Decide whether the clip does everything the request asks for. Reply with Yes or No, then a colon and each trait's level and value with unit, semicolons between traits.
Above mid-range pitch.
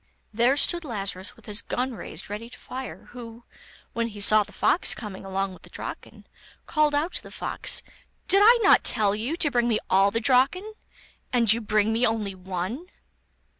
Yes: high, 230 Hz